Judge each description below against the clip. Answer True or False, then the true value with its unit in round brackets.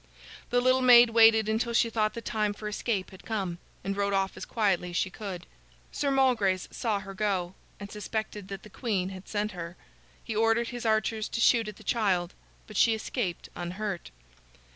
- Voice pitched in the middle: False (210 Hz)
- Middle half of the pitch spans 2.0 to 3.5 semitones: True (2.9 semitones)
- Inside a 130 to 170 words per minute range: False (190 wpm)